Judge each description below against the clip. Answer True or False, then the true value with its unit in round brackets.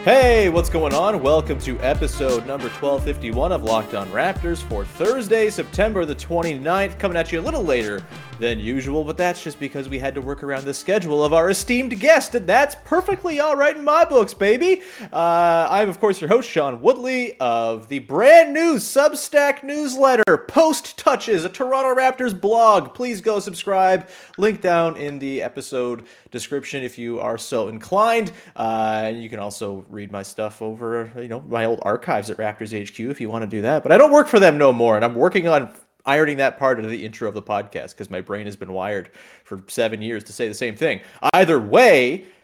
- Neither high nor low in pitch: True (160 Hz)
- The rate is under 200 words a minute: False (205 wpm)